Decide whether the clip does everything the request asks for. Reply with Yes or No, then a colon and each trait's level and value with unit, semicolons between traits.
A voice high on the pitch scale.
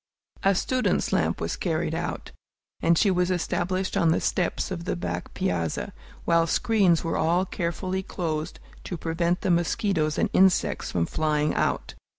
No: medium, 170 Hz